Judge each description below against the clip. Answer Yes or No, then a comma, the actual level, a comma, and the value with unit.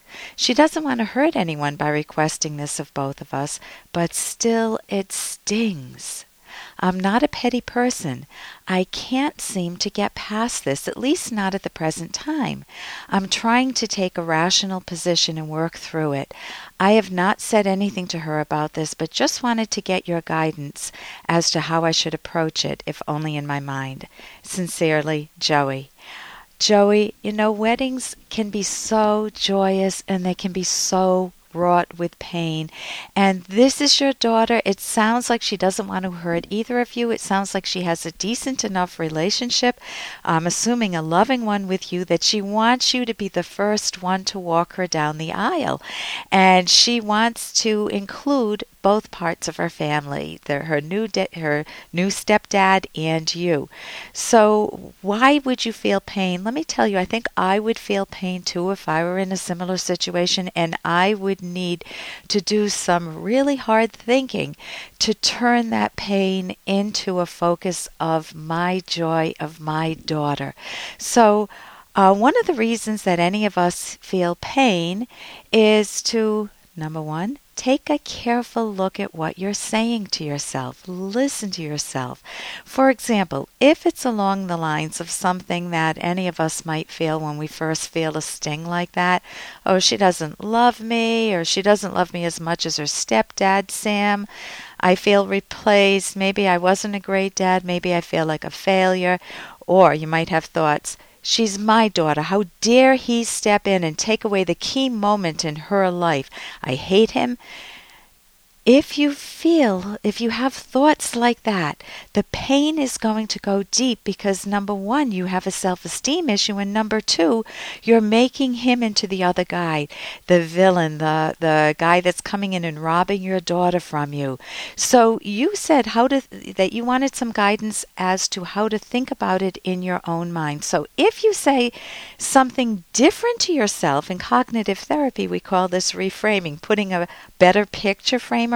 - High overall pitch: Yes, high, 195 Hz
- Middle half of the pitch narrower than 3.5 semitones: No, average, 4.8 semitones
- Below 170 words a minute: No, average, 175 wpm